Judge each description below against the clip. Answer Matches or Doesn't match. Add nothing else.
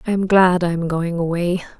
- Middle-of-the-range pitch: Matches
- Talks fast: Matches